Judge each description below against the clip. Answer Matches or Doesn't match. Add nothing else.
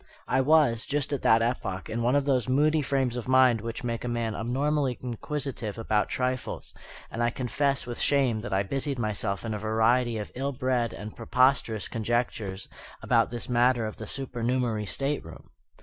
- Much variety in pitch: Doesn't match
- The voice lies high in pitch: Doesn't match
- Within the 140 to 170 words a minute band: Doesn't match